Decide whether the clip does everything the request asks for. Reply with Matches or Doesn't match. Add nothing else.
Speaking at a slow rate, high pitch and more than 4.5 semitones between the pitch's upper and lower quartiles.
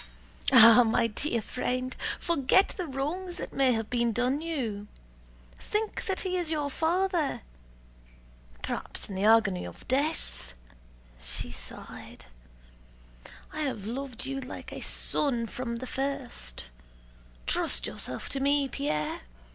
Matches